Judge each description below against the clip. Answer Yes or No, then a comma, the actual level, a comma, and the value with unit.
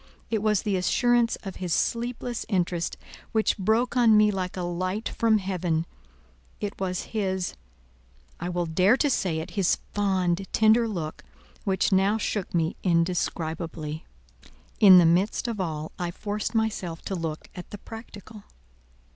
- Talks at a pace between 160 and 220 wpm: No, average, 145 wpm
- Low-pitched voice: No, high, 190 Hz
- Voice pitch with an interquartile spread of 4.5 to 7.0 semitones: No, average, 3.9 semitones